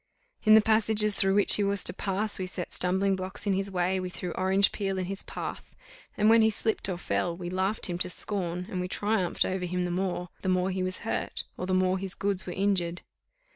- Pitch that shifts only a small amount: Yes, narrow, 1.8 semitones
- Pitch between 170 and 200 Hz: Yes, high, 190 Hz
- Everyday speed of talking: No, fast, 235 wpm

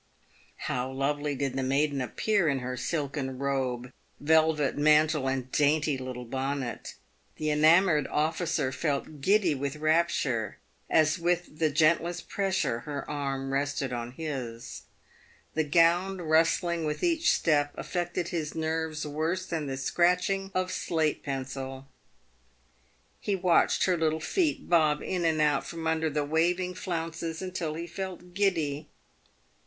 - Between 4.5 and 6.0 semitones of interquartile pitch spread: No, average, 3.6 semitones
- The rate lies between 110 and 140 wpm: Yes, slow, 135 wpm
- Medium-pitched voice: Yes, medium, 155 Hz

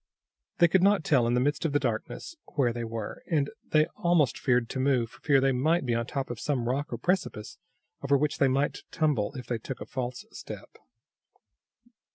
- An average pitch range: Yes, average, 3.7 semitones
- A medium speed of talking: No, fast, 210 wpm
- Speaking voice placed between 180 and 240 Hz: No, low, 135 Hz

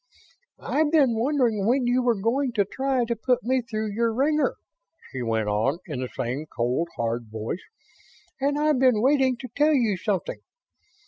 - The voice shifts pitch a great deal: Yes, wide, 8.0 semitones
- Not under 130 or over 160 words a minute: No, average, 175 wpm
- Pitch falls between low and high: No, high, 235 Hz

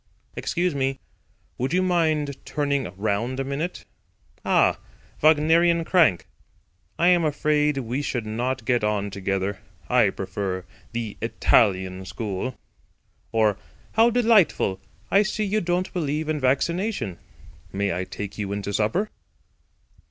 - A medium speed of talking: No, slow, 125 wpm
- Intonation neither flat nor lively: No, wide, 8.5 semitones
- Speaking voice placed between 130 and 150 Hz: Yes, low, 135 Hz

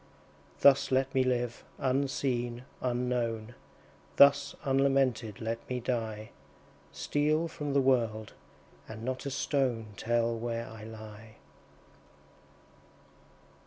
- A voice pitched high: No, low, 125 Hz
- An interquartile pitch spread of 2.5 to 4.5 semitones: Yes, average, 3.0 semitones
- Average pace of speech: No, slow, 100 wpm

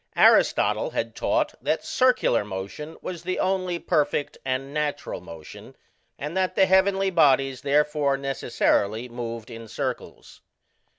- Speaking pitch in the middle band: Yes, medium, 145 Hz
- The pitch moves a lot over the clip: Yes, wide, 7.0 semitones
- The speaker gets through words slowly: Yes, slow, 125 wpm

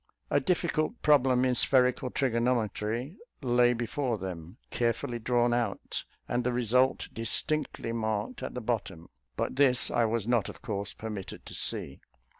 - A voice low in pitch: Yes, low, 120 Hz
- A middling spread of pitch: No, narrow, 2.2 semitones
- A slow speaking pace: No, average, 145 wpm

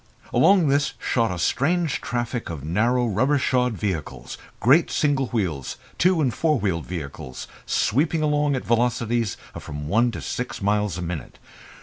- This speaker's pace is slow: No, average, 155 wpm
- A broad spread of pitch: Yes, wide, 7.0 semitones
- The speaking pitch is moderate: No, low, 120 Hz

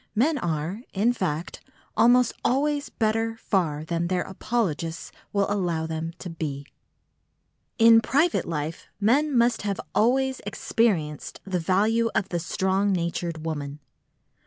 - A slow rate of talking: Yes, slow, 130 wpm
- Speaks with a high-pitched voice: Yes, high, 195 Hz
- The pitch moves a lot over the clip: Yes, wide, 5.8 semitones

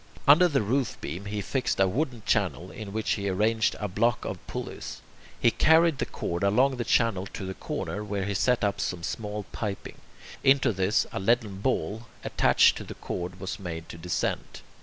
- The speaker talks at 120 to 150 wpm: No, average, 190 wpm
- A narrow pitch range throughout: No, average, 3.8 semitones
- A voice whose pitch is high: No, low, 105 Hz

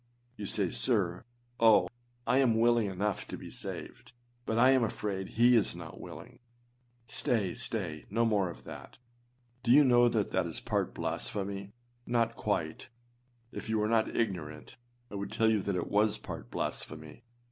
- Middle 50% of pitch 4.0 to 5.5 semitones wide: No, average, 3.2 semitones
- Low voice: Yes, low, 105 Hz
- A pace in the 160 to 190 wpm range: Yes, average, 170 wpm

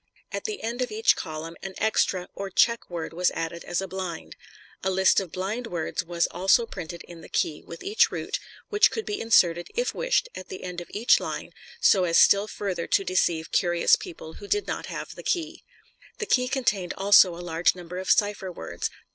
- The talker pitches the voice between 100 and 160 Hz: No, medium, 185 Hz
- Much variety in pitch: No, average, 4.7 semitones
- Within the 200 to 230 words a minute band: Yes, fast, 205 wpm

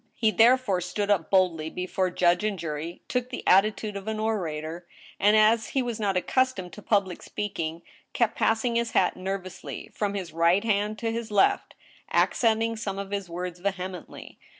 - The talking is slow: No, average, 175 wpm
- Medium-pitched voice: No, high, 200 Hz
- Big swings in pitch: No, average, 3.5 semitones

